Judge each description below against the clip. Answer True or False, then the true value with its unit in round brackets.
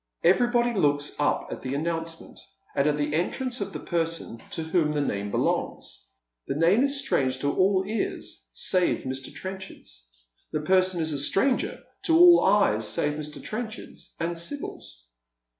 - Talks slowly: False (160 wpm)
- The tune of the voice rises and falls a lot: True (5.7 semitones)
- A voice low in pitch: False (165 Hz)